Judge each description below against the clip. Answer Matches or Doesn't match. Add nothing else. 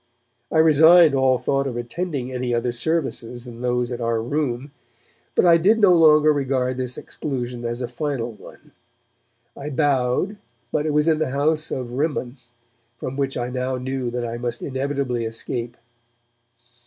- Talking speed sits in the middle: Matches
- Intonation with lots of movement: Doesn't match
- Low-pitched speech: Matches